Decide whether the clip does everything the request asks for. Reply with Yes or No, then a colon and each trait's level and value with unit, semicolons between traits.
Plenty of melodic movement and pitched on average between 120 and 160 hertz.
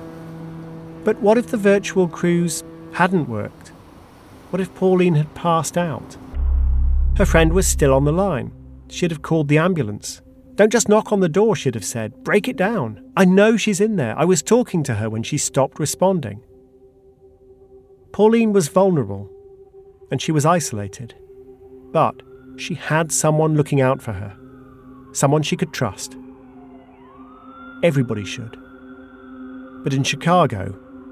Yes: wide, 5.7 semitones; medium, 140 Hz